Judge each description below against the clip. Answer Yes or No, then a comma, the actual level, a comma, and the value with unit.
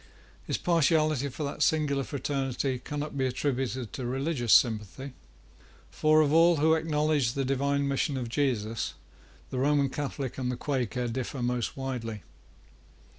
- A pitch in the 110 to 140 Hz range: Yes, low, 135 Hz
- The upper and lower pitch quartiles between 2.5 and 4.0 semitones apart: Yes, average, 2.9 semitones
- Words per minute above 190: No, average, 140 wpm